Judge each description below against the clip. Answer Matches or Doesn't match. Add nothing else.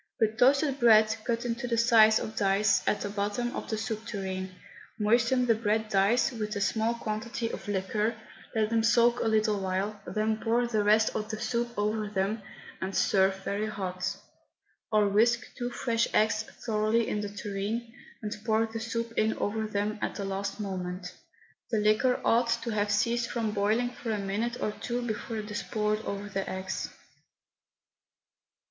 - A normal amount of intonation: Doesn't match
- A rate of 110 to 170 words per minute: Doesn't match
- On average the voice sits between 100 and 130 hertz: Doesn't match